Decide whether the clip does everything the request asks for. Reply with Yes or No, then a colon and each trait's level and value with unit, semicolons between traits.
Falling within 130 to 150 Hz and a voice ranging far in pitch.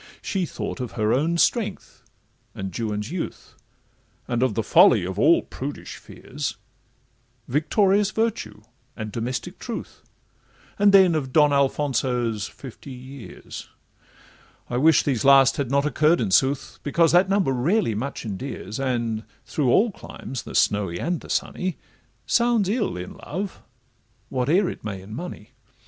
Yes: low, 135 Hz; wide, 6.8 semitones